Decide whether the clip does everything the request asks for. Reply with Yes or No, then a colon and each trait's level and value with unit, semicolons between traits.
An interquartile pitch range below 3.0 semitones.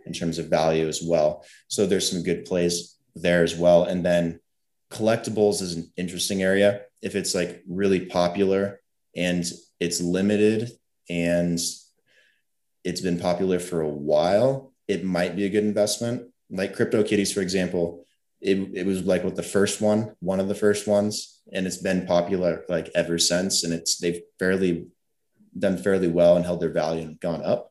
Yes: narrow, 2.6 semitones